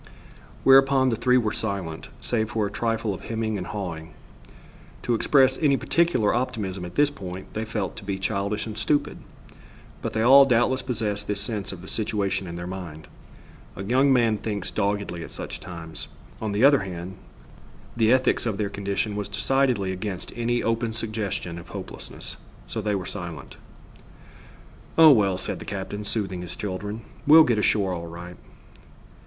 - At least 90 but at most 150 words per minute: No, average, 170 wpm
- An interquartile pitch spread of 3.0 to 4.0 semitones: Yes, average, 3.7 semitones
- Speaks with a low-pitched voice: Yes, low, 105 Hz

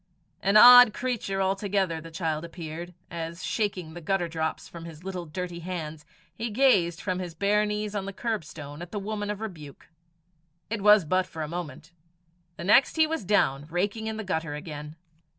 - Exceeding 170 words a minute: Yes, average, 185 wpm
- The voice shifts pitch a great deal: No, average, 4.3 semitones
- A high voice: No, medium, 180 Hz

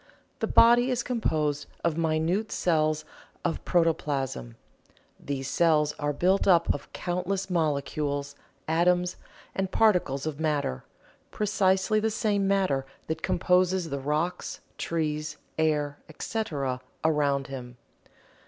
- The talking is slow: Yes, slow, 115 wpm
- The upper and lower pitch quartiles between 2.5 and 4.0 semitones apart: No, average, 4.4 semitones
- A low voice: No, medium, 160 Hz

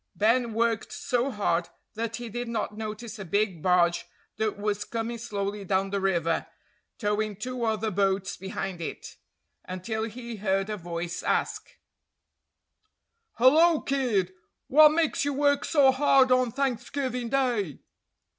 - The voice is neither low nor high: No, high, 220 Hz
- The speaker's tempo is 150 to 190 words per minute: No, slow, 135 wpm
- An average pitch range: Yes, average, 4.4 semitones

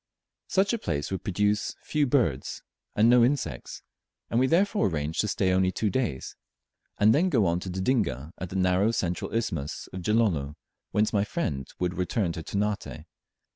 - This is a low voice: Yes, low, 100 Hz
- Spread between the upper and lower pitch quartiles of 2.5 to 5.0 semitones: No, wide, 5.4 semitones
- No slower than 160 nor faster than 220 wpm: Yes, average, 175 wpm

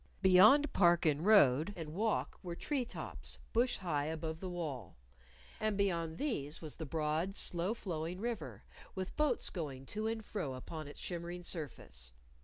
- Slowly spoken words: No, average, 160 wpm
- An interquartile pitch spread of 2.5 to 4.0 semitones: No, average, 4.9 semitones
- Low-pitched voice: No, medium, 170 Hz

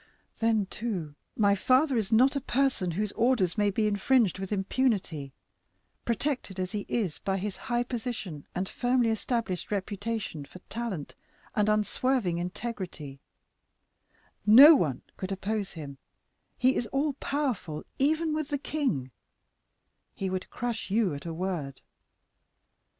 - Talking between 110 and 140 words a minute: Yes, slow, 135 wpm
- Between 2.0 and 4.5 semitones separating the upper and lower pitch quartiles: No, average, 5.0 semitones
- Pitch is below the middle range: No, high, 210 Hz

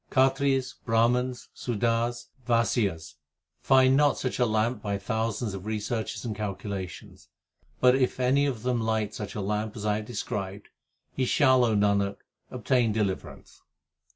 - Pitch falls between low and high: No, low, 115 Hz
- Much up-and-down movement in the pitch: No, average, 3.3 semitones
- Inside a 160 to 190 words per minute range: No, average, 150 wpm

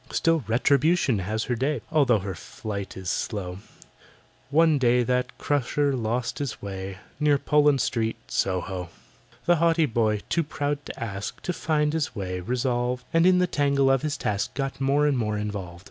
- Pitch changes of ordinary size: No, wide, 5.8 semitones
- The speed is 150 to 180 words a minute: Yes, average, 170 wpm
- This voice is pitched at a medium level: No, low, 125 Hz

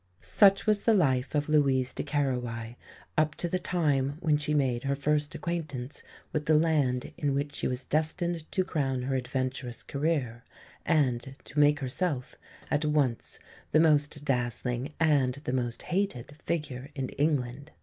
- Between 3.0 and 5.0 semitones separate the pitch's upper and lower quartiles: Yes, average, 3.3 semitones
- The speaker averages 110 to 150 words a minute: No, average, 160 wpm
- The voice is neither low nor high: Yes, medium, 145 Hz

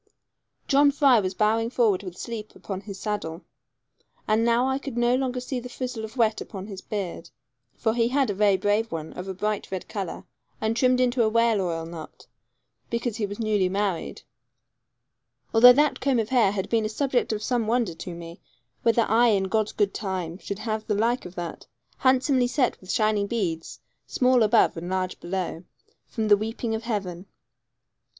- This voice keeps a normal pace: Yes, average, 190 wpm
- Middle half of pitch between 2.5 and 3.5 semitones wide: No, average, 3.9 semitones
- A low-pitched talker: No, high, 215 Hz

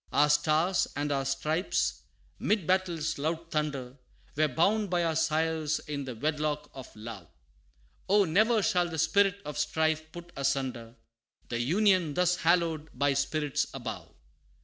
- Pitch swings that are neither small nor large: Yes, average, 3.5 semitones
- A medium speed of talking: Yes, average, 145 wpm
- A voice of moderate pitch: Yes, medium, 155 Hz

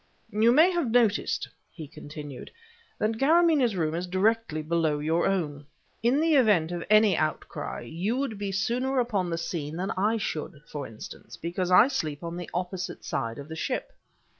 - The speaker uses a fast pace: No, average, 175 wpm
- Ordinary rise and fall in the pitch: No, wide, 6.3 semitones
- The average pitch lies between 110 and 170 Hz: No, medium, 185 Hz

